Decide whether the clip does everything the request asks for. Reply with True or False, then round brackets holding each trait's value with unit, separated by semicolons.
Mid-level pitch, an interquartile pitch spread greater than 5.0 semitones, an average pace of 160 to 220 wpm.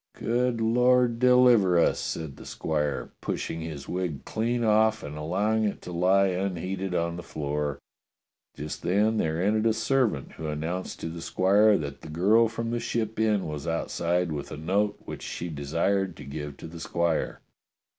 False (90 Hz; 5.5 semitones; 175 wpm)